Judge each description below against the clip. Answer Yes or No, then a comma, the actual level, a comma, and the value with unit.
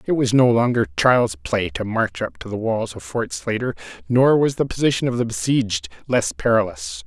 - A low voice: Yes, low, 120 Hz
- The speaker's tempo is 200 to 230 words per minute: Yes, fast, 205 wpm